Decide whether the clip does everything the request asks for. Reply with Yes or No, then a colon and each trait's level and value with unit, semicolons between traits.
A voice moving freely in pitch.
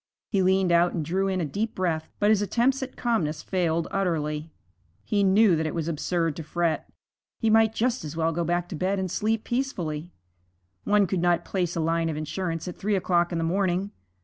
No: average, 3.5 semitones